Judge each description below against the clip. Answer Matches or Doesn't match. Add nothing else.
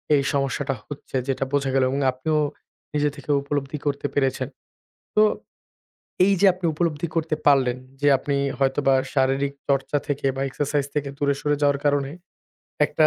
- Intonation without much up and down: Matches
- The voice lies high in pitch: Doesn't match